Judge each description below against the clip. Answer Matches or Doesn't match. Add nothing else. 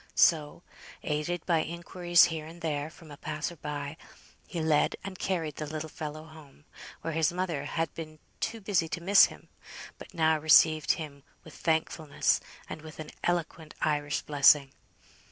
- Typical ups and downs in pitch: Doesn't match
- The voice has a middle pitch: Matches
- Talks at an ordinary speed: Matches